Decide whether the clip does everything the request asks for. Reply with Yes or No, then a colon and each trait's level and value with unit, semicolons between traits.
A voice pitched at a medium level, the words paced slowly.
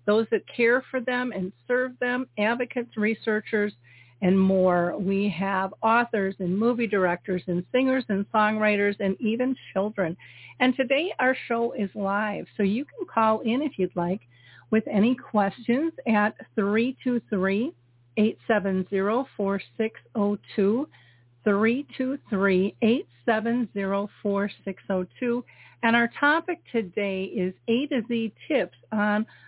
No: high, 215 Hz; slow, 110 wpm